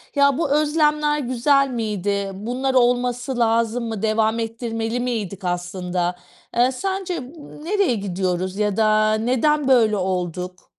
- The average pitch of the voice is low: No, high, 230 Hz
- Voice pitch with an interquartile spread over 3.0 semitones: Yes, average, 4.8 semitones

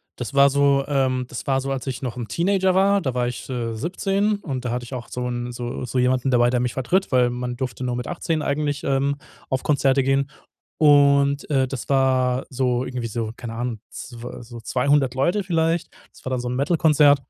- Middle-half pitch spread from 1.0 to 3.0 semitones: Yes, narrow, 2.5 semitones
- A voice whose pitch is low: Yes, low, 130 Hz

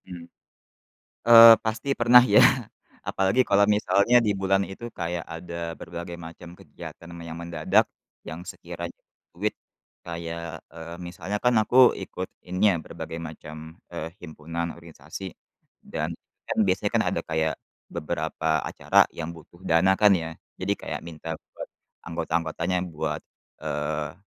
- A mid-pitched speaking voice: No, very low, 85 Hz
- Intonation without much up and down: No, average, 3.1 semitones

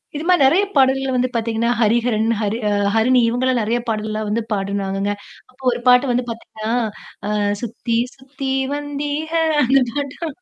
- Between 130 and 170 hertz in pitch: No, high, 245 Hz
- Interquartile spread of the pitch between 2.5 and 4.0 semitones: Yes, average, 3.5 semitones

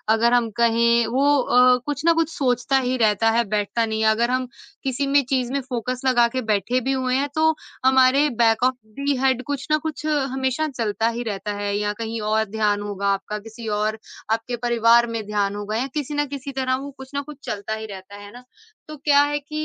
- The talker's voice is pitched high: Yes, high, 240 Hz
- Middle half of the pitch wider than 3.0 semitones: Yes, average, 3.7 semitones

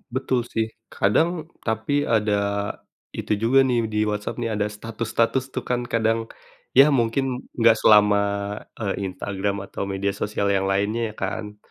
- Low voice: Yes, low, 110 Hz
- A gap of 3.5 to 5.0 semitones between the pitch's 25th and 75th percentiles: No, narrow, 2.6 semitones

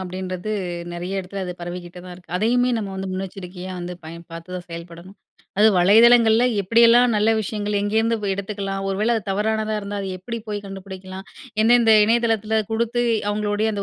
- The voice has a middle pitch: No, high, 200 Hz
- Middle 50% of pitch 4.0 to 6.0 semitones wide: No, average, 3.2 semitones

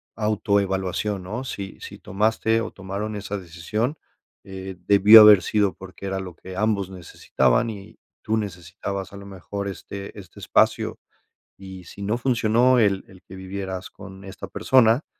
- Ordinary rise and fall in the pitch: No, narrow, 2.2 semitones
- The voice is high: No, low, 100 Hz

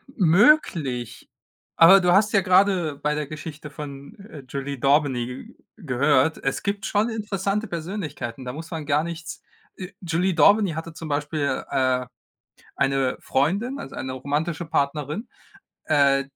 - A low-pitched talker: No, medium, 155 Hz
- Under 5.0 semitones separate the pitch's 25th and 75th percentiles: No, average, 5.3 semitones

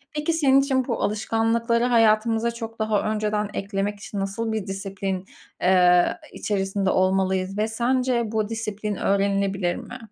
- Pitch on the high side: Yes, high, 215 Hz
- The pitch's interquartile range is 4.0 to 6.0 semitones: No, average, 2.8 semitones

